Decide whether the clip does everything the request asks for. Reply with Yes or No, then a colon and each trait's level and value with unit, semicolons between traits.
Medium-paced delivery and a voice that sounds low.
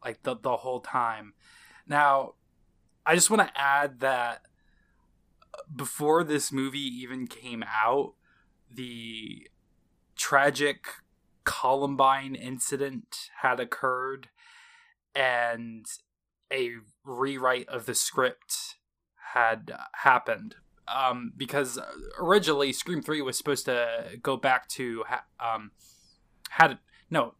No: slow, 105 wpm; low, 130 Hz